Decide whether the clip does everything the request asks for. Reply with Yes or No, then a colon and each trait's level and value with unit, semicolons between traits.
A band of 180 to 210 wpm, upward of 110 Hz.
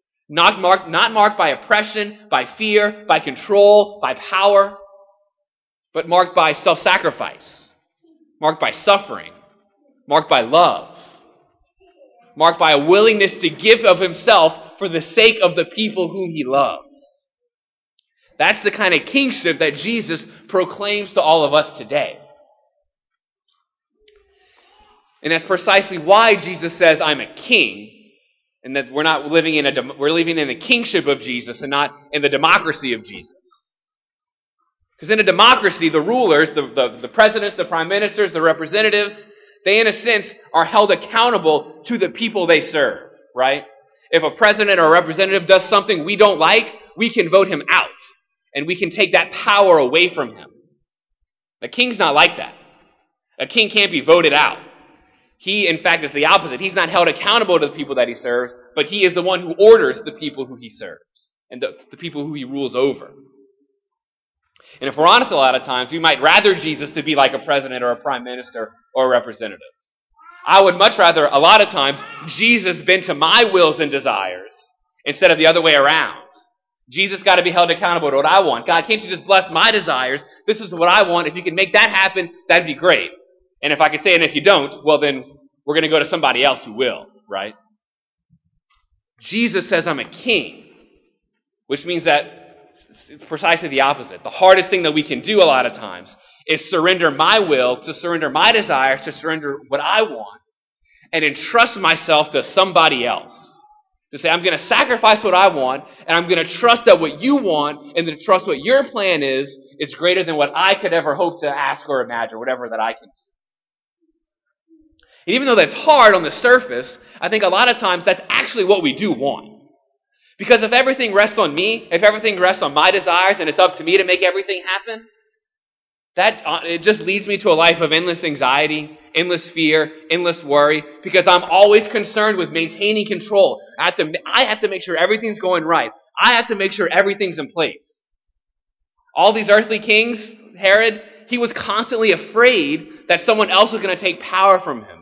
Yes: average, 195 wpm; high, 190 Hz